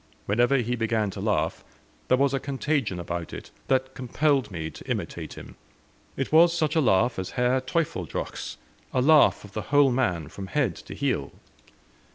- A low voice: Yes, low, 125 Hz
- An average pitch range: No, wide, 5.7 semitones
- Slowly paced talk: No, average, 175 wpm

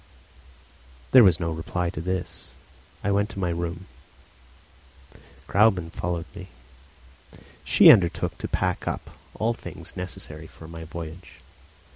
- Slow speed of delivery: Yes, slow, 130 wpm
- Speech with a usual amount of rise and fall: No, narrow, 2.3 semitones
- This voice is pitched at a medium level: No, very low, 90 Hz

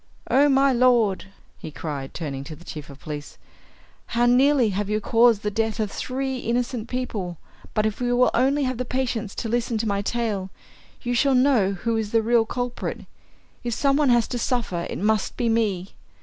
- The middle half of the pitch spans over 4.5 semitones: No, average, 3.7 semitones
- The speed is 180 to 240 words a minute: Yes, average, 195 wpm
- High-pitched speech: Yes, high, 230 Hz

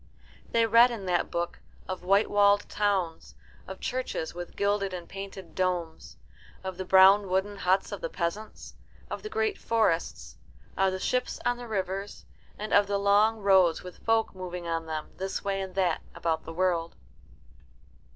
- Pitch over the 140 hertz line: Yes, high, 190 Hz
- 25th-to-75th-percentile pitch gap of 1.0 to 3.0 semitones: Yes, narrow, 2.5 semitones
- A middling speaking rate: Yes, average, 170 wpm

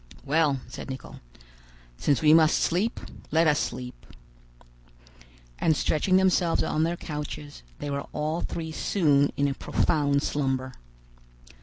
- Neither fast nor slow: No, slow, 130 wpm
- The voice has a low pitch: No, medium, 150 Hz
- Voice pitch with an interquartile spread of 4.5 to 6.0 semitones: No, narrow, 2.5 semitones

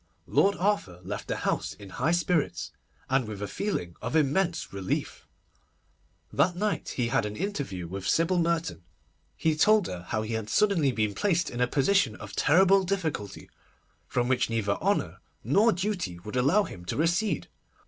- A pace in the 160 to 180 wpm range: Yes, average, 170 wpm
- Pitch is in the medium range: Yes, medium, 145 Hz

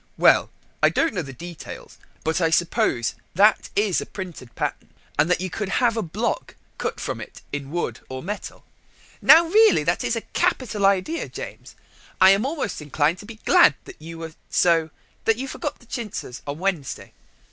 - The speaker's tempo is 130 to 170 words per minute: No, average, 185 wpm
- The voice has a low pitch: No, medium, 185 Hz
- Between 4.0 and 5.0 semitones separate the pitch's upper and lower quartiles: No, wide, 5.6 semitones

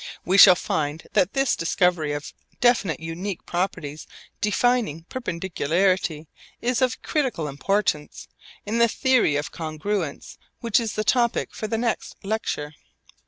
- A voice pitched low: No, high, 190 Hz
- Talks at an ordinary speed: No, slow, 130 wpm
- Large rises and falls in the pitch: Yes, wide, 6.4 semitones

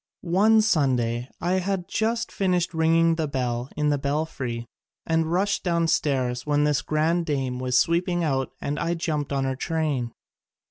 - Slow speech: No, average, 160 wpm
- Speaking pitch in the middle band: Yes, medium, 155 Hz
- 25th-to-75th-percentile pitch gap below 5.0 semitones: Yes, average, 4.4 semitones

